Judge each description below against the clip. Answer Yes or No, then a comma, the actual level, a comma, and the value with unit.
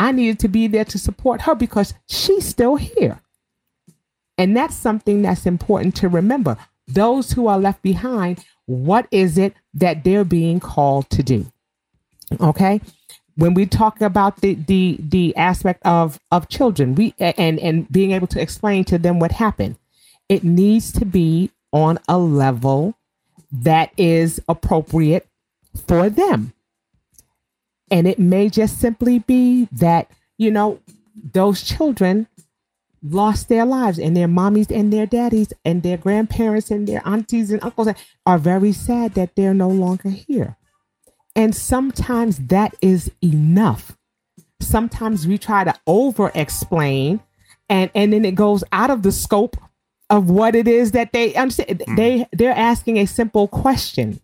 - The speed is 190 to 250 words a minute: No, average, 155 wpm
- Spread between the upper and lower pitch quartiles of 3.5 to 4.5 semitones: Yes, average, 4.1 semitones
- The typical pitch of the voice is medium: No, high, 195 Hz